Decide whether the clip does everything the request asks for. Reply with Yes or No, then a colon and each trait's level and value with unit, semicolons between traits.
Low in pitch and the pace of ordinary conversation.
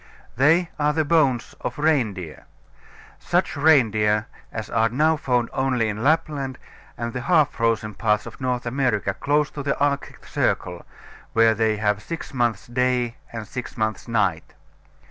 Yes: low, 125 Hz; average, 150 wpm